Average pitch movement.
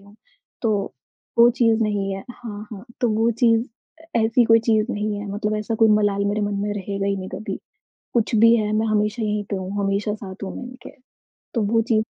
No: narrow, 1.9 semitones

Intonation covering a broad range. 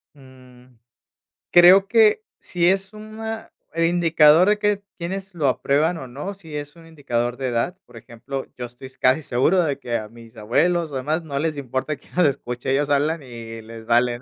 Yes: wide, 5.9 semitones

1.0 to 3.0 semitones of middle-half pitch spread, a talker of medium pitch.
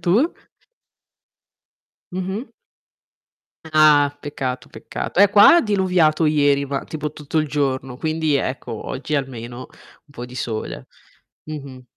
No: average, 3.4 semitones; medium, 145 Hz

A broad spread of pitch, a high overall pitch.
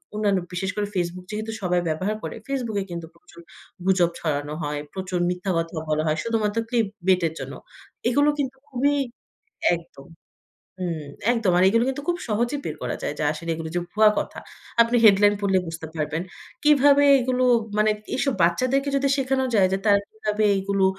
Yes: wide, 5.9 semitones; high, 200 Hz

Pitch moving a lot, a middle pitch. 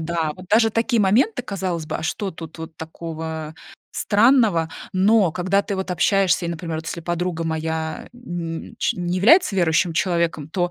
No: average, 3.5 semitones; medium, 175 Hz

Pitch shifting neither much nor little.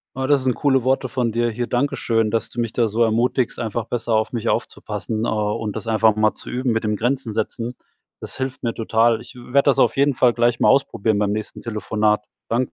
No: narrow, 2.3 semitones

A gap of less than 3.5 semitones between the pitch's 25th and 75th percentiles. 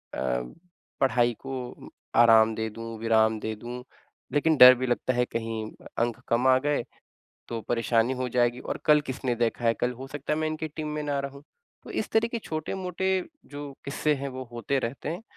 No: average, 4.0 semitones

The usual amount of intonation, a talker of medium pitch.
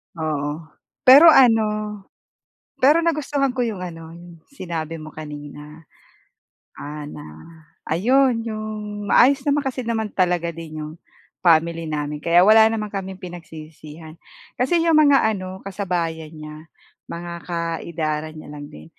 No: wide, 6.0 semitones; medium, 175 Hz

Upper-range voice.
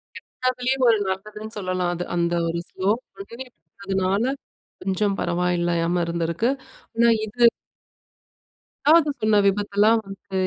Yes: high, 195 Hz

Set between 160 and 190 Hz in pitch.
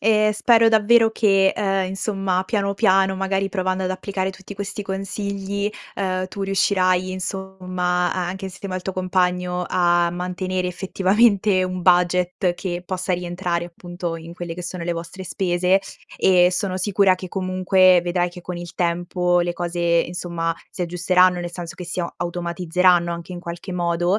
Yes: medium, 185 Hz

